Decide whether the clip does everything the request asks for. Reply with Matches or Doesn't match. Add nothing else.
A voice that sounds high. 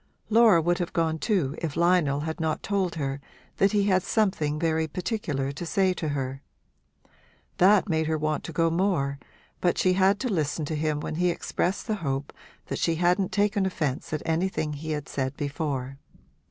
Doesn't match